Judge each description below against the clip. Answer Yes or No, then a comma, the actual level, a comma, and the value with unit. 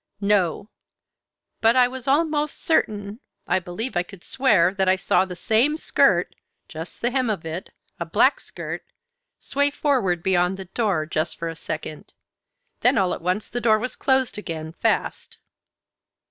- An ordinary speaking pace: Yes, average, 160 wpm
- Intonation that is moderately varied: No, wide, 6.2 semitones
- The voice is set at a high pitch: Yes, high, 200 Hz